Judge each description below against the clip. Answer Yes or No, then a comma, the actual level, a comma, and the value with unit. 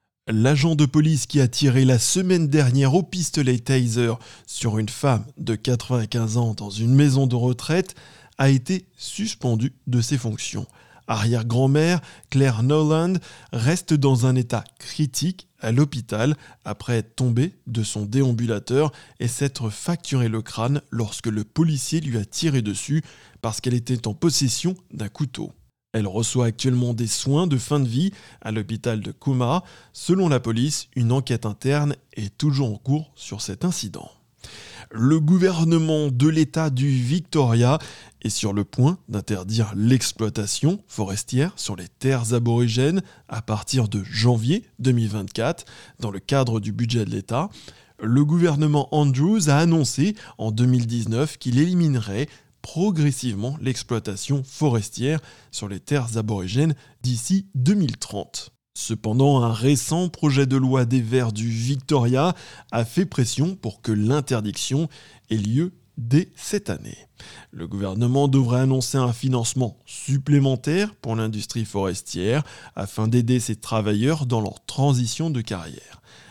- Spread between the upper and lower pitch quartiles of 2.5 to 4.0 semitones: No, average, 4.6 semitones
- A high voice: No, low, 130 Hz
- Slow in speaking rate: Yes, slow, 140 wpm